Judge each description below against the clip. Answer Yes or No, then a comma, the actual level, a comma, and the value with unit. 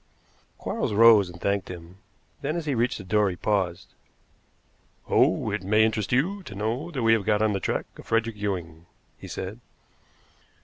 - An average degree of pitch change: Yes, average, 3.3 semitones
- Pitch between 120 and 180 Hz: No, low, 105 Hz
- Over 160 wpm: Yes, average, 180 wpm